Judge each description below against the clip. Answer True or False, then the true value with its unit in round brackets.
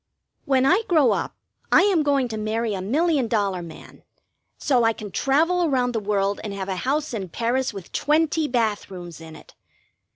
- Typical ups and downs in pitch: False (6.4 semitones)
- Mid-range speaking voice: False (235 Hz)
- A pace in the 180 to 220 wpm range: True (190 wpm)